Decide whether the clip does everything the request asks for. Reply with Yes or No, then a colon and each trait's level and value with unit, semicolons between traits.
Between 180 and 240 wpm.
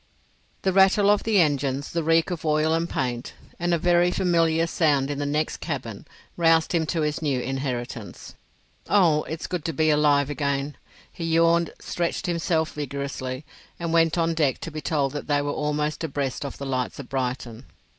Yes: average, 185 wpm